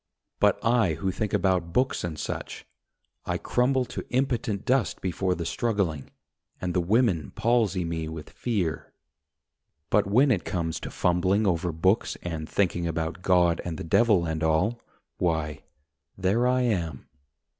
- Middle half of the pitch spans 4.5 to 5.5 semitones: Yes, average, 5.2 semitones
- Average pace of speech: Yes, average, 150 wpm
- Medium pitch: No, very low, 90 Hz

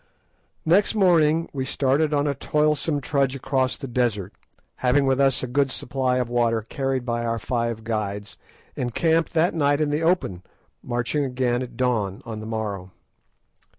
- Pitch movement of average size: Yes, average, 3.8 semitones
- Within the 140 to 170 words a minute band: Yes, average, 165 wpm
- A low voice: Yes, low, 130 Hz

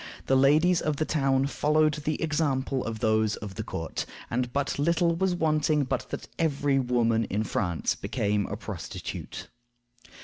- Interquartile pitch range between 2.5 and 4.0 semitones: No, average, 5.3 semitones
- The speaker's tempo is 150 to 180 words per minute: Yes, average, 160 wpm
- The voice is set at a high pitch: No, low, 135 Hz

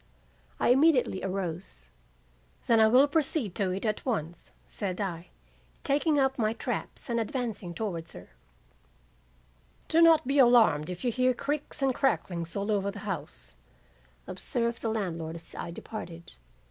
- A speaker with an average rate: Yes, average, 145 wpm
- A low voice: No, high, 215 Hz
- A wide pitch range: Yes, wide, 6.4 semitones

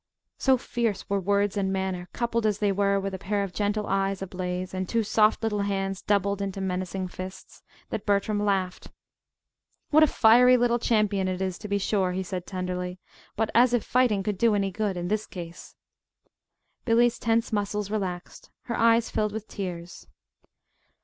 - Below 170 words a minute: No, average, 175 wpm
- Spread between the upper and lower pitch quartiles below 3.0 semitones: Yes, narrow, 2.5 semitones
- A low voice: No, high, 200 Hz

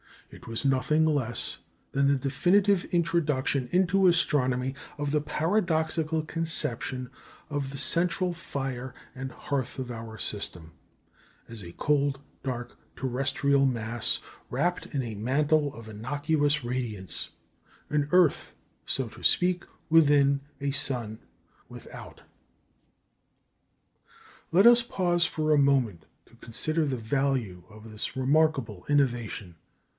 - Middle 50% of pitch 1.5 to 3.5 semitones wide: No, average, 4.3 semitones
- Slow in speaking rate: Yes, slow, 120 wpm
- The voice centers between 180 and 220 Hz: No, medium, 140 Hz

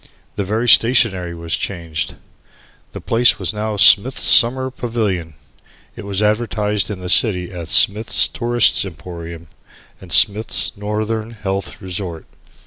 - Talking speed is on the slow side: Yes, slow, 130 wpm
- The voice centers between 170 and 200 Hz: No, low, 105 Hz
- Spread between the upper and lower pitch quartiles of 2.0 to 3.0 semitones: No, average, 3.8 semitones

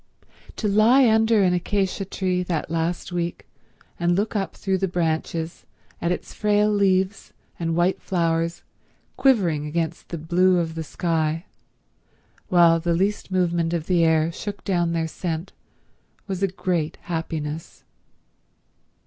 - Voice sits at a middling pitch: Yes, medium, 175 Hz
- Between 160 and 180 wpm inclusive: No, average, 140 wpm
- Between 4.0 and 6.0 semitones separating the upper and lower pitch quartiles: No, narrow, 2.6 semitones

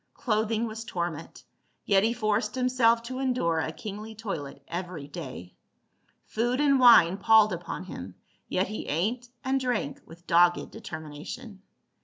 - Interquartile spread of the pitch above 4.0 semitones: Yes, wide, 5.6 semitones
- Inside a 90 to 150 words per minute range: Yes, average, 140 wpm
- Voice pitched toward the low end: No, high, 210 Hz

